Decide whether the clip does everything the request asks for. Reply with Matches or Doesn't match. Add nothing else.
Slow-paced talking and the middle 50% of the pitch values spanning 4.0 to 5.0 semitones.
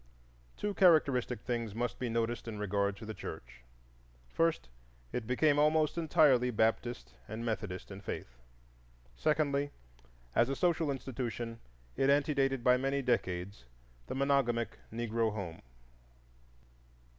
Matches